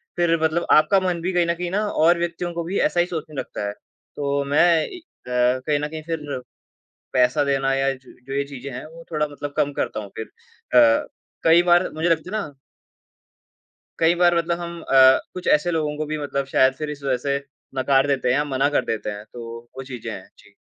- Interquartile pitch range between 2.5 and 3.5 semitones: No, average, 4.0 semitones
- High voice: No, medium, 150 Hz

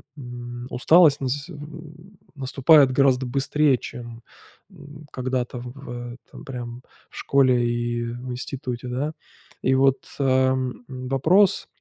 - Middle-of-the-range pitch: No, low, 130 Hz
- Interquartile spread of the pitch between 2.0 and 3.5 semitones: Yes, average, 2.8 semitones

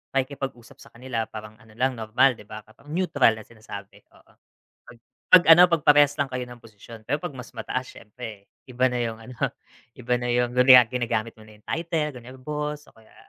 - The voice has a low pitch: Yes, low, 125 Hz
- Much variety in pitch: No, average, 3.9 semitones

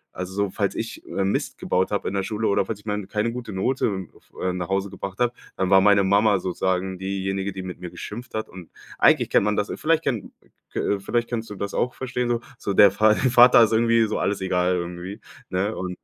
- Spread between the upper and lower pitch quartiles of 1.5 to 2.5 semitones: No, average, 2.9 semitones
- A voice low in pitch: Yes, low, 100 Hz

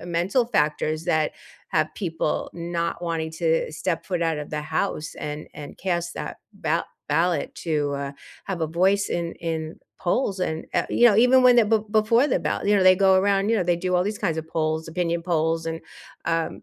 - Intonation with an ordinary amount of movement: Yes, average, 3.4 semitones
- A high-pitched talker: No, medium, 170 Hz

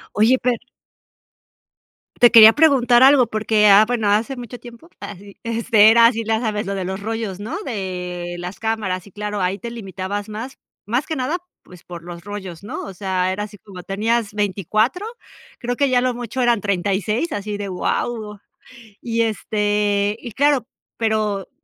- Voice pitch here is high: Yes, high, 215 Hz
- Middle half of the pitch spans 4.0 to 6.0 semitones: No, average, 3.1 semitones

